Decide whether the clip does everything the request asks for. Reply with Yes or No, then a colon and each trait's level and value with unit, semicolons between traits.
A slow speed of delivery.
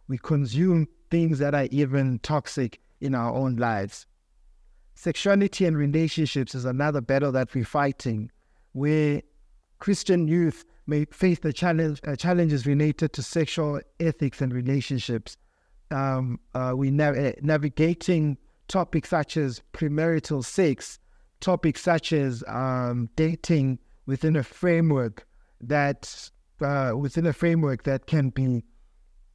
Yes: slow, 125 wpm